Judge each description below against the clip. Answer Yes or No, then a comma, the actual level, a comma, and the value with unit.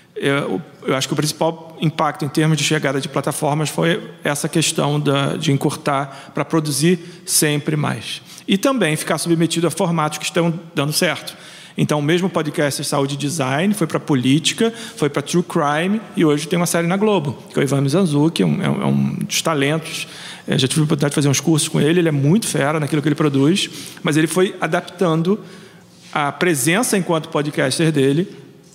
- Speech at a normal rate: No, fast, 195 wpm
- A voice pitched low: No, medium, 160 Hz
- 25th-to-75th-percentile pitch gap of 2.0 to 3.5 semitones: Yes, average, 3.1 semitones